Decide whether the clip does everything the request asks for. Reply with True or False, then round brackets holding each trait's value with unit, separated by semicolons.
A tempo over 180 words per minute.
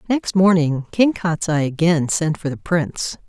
False (165 wpm)